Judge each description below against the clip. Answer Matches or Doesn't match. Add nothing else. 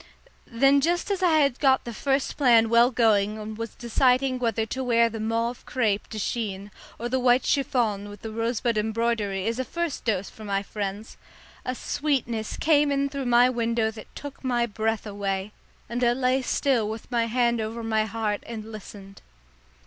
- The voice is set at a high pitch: Matches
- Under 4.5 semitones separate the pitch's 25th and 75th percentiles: Matches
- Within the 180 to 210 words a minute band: Matches